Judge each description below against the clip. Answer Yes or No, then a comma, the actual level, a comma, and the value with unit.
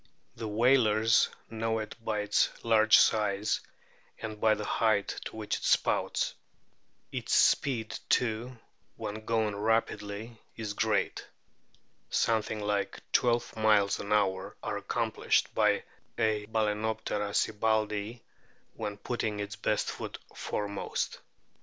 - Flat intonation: Yes, narrow, 1.3 semitones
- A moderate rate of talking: No, slow, 115 wpm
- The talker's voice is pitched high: No, low, 110 Hz